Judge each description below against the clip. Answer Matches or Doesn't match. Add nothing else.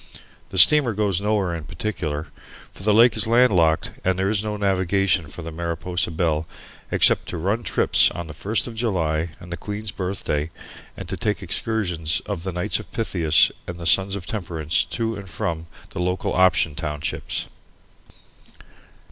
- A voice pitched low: Matches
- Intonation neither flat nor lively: Matches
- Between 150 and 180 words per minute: Matches